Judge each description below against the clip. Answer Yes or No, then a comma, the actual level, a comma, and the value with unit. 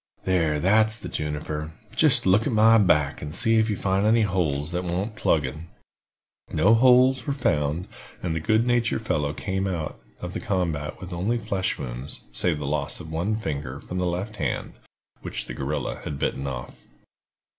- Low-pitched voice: Yes, very low, 90 Hz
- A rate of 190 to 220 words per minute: No, average, 180 wpm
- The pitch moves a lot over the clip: Yes, wide, 6.2 semitones